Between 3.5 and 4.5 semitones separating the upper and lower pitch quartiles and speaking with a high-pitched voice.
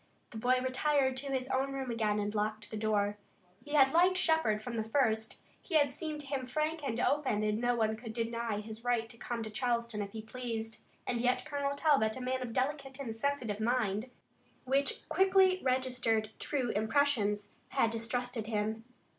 Yes: average, 3.9 semitones; high, 245 Hz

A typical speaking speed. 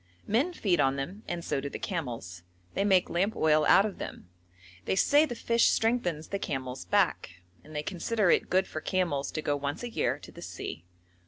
No: fast, 210 wpm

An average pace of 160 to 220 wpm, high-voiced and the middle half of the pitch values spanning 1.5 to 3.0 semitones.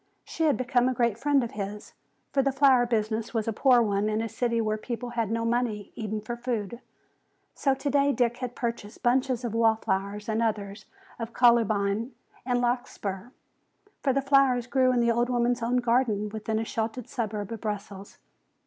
Yes: average, 185 wpm; high, 235 Hz; narrow, 2.5 semitones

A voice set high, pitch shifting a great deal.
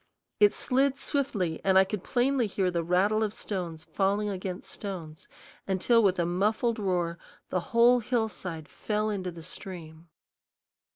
No: high, 195 Hz; average, 3.7 semitones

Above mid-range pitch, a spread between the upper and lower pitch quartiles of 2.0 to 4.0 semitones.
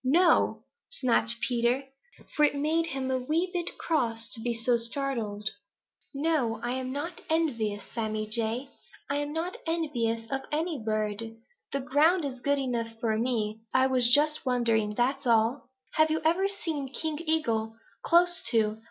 No: very high, 260 Hz; average, 5.2 semitones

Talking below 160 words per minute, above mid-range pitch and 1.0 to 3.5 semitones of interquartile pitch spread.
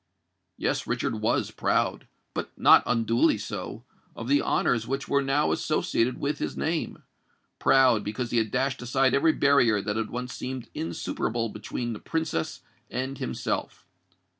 No: average, 140 wpm; low, 125 Hz; average, 3.2 semitones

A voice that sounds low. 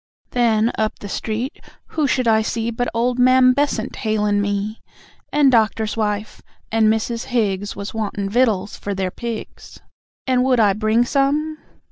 No: high, 225 Hz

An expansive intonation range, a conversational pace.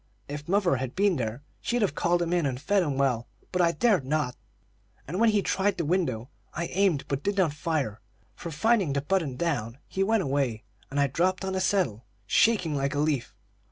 No: wide, 5.7 semitones; fast, 210 wpm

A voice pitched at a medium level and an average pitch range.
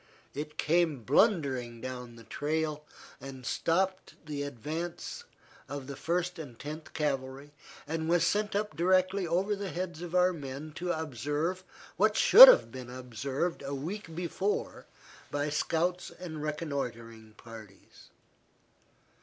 Yes: medium, 155 Hz; average, 4.7 semitones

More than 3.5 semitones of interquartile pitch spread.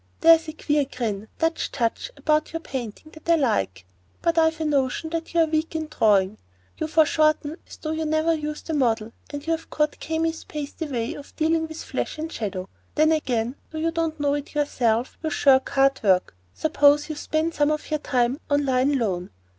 Yes: average, 3.9 semitones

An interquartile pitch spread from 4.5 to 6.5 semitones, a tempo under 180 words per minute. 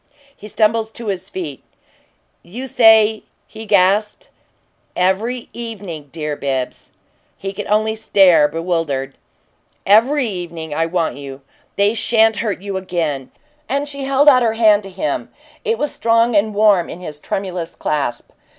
Yes: average, 5.0 semitones; average, 150 wpm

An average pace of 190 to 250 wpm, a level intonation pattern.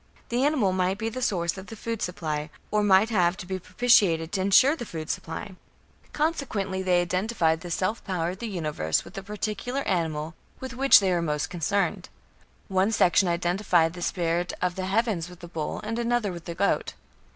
No: average, 195 wpm; average, 3.9 semitones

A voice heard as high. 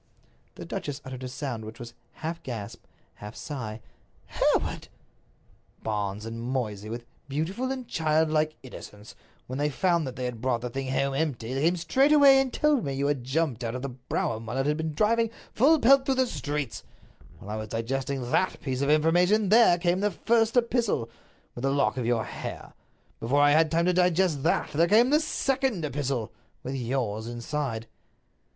No: medium, 140 Hz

